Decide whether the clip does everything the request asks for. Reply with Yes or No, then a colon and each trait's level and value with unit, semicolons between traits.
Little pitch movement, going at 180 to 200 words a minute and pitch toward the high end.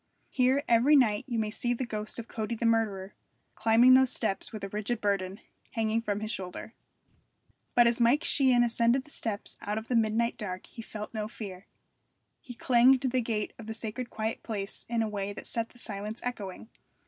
Yes: narrow, 2.3 semitones; average, 195 wpm; high, 225 Hz